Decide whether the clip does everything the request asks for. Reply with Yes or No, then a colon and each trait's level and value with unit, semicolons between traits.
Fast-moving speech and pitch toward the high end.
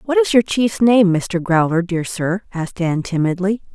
No: average, 190 wpm; high, 195 Hz